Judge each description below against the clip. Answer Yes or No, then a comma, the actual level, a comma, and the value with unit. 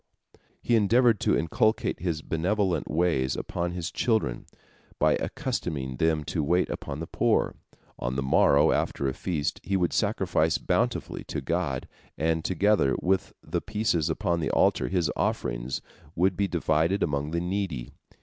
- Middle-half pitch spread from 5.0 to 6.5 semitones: No, average, 4.5 semitones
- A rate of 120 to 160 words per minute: Yes, average, 150 wpm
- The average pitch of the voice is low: Yes, very low, 85 Hz